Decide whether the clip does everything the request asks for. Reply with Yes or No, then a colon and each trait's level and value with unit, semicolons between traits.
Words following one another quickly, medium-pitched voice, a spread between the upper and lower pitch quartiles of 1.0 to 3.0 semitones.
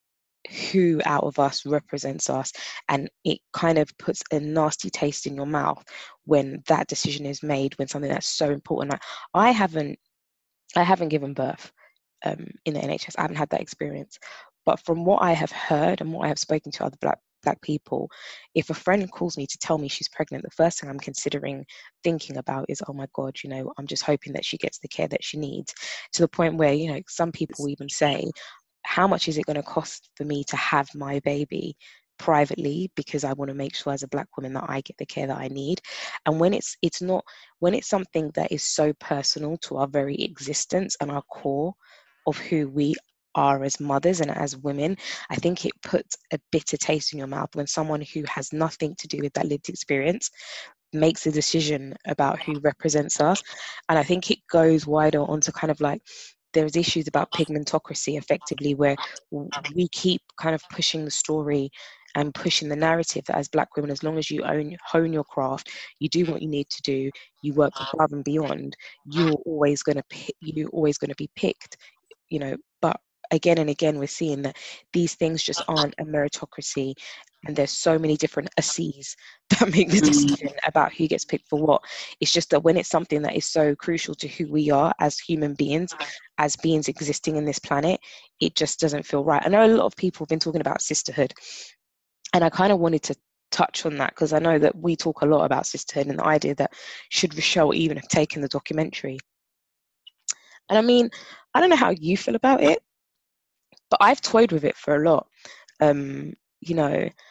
Yes: fast, 210 wpm; medium, 150 Hz; narrow, 2.4 semitones